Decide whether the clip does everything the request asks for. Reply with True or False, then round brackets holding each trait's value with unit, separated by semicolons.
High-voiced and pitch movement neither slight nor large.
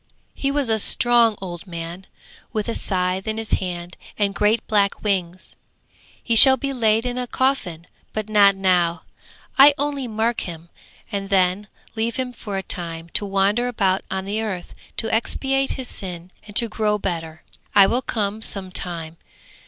True (205 Hz; 4.1 semitones)